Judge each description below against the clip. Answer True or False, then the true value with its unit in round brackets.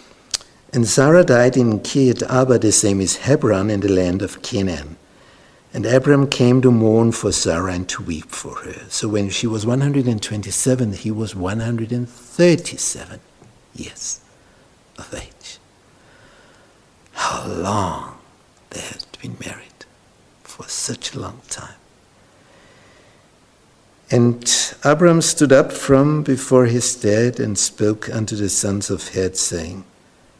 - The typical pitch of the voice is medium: False (115 Hz)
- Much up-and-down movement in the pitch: False (4.3 semitones)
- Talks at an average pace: False (130 wpm)